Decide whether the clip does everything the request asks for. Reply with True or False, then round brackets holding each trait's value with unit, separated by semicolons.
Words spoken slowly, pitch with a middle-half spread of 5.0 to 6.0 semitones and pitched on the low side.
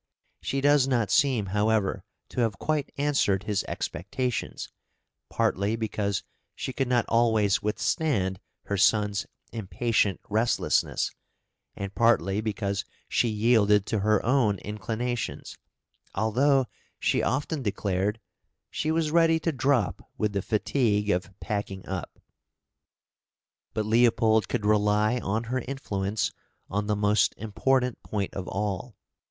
False (125 wpm; 3.4 semitones; 110 Hz)